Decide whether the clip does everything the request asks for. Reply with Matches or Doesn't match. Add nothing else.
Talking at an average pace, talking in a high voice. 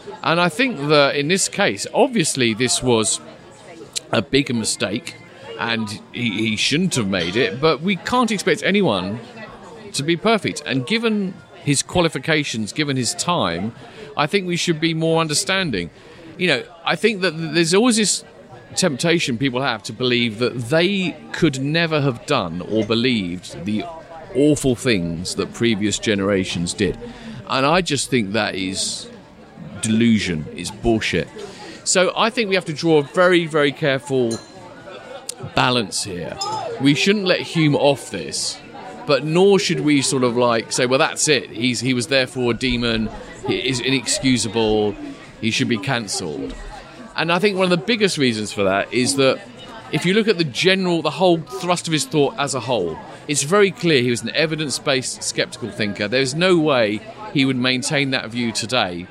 Doesn't match